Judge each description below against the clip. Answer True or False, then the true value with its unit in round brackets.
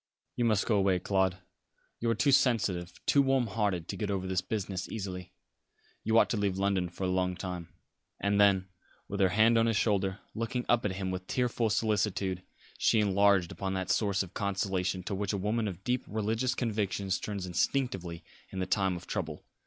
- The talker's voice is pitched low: True (100 Hz)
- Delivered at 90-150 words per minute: False (195 wpm)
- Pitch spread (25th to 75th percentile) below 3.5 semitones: True (2.9 semitones)